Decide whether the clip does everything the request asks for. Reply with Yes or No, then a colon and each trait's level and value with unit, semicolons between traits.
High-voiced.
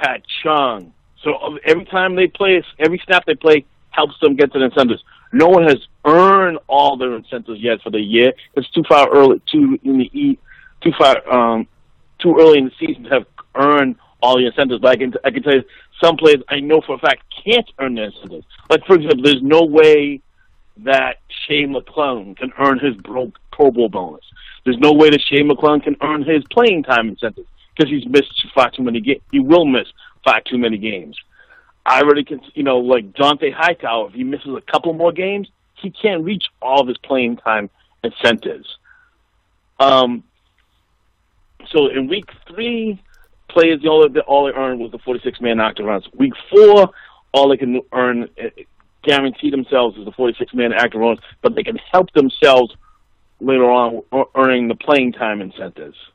No: medium, 140 Hz